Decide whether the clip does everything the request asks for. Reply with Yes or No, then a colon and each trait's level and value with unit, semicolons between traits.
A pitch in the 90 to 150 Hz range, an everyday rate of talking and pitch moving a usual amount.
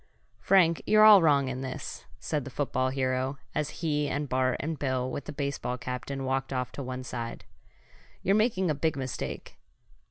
Yes: medium, 140 Hz; average, 180 wpm; average, 3.1 semitones